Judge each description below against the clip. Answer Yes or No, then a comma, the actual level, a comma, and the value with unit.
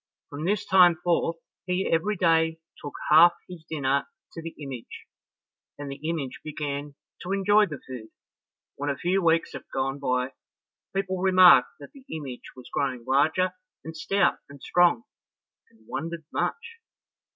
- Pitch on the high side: No, medium, 160 Hz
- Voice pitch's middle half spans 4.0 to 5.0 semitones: Yes, average, 4.4 semitones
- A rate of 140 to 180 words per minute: Yes, average, 150 wpm